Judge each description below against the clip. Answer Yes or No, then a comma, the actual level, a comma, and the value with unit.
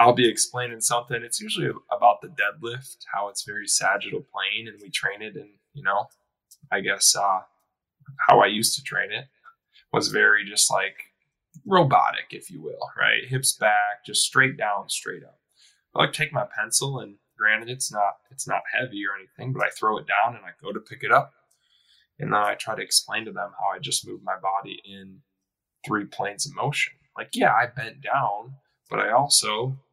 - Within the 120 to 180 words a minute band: No, average, 200 wpm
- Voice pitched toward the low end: Yes, low, 120 Hz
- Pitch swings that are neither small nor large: Yes, average, 4.5 semitones